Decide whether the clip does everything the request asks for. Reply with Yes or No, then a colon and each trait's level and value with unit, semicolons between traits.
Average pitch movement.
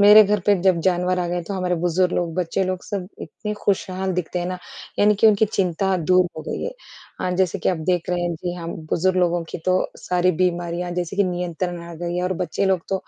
No: narrow, 1.5 semitones